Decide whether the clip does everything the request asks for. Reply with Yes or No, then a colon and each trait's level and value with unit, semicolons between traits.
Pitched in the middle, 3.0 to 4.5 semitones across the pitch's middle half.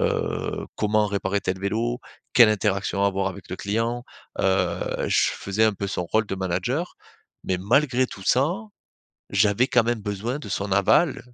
No: low, 105 Hz; average, 3.5 semitones